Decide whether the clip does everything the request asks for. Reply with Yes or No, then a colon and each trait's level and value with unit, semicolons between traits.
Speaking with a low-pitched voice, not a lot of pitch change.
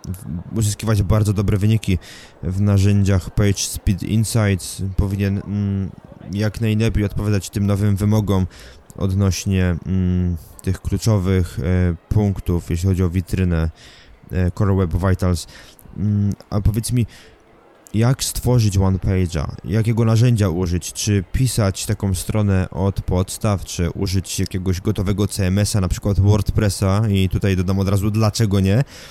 Yes: low, 100 Hz; narrow, 2.3 semitones